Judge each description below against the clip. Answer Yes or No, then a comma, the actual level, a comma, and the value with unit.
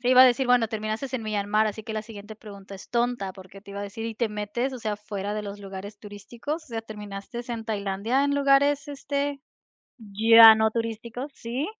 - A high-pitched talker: Yes, high, 220 Hz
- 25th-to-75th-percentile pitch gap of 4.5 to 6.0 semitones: No, average, 3.1 semitones